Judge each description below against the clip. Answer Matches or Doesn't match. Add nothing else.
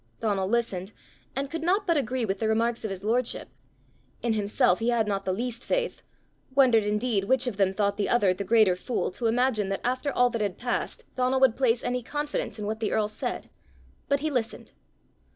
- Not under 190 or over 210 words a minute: Matches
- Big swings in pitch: Doesn't match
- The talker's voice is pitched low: Doesn't match